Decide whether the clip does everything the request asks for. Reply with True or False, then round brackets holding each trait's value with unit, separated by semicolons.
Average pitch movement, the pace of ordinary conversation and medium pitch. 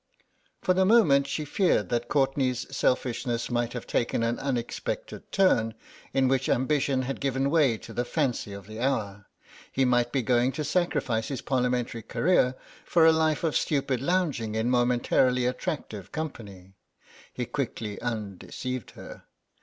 False (3.2 semitones; 150 wpm; 125 Hz)